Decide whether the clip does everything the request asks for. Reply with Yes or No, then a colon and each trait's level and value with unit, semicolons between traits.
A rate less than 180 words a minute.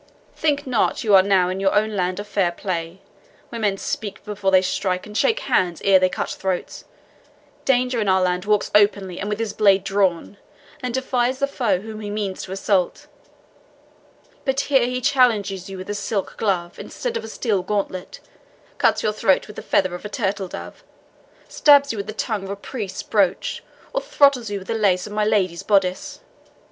No: average, 200 wpm